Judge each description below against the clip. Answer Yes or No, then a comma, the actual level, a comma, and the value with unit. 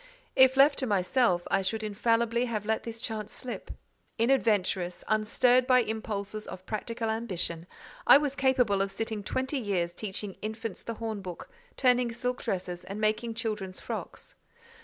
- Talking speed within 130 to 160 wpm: Yes, average, 150 wpm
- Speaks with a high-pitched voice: Yes, high, 220 Hz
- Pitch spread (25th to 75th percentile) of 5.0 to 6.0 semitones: No, average, 3.5 semitones